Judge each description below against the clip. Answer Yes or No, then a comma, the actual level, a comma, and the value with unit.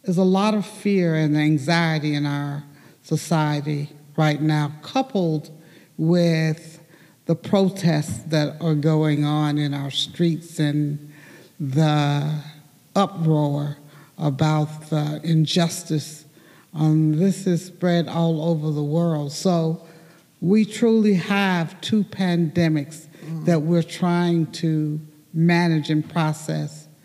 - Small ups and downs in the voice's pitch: Yes, narrow, 2.2 semitones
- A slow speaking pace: Yes, slow, 110 wpm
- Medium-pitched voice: Yes, medium, 160 Hz